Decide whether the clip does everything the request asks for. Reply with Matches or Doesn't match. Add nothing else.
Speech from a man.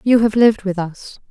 Doesn't match